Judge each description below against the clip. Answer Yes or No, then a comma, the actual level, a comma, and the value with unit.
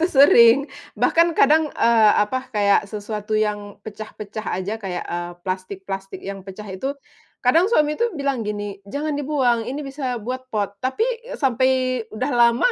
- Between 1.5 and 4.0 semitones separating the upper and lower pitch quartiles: No, average, 4.8 semitones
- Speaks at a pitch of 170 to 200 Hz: No, high, 230 Hz